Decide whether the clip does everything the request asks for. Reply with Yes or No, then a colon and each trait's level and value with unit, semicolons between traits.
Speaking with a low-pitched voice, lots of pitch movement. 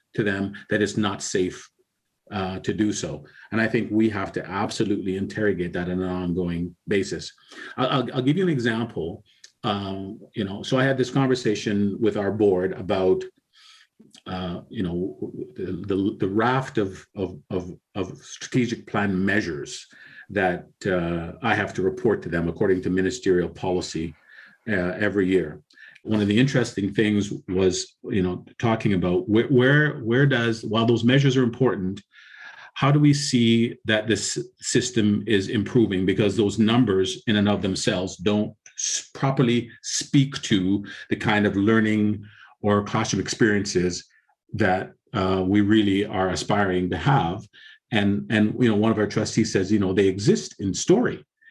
No: low, 105 Hz; average, 3.6 semitones